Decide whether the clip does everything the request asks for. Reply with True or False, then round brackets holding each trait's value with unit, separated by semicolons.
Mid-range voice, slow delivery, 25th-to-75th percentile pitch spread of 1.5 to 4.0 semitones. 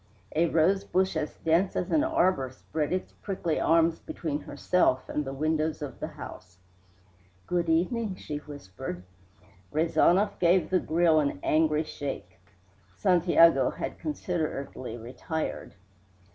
True (160 Hz; 125 wpm; 3.5 semitones)